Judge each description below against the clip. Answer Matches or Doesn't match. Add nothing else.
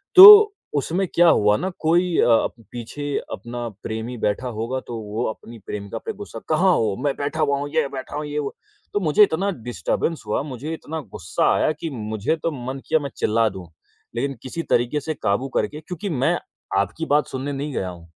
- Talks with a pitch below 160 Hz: Matches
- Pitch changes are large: Matches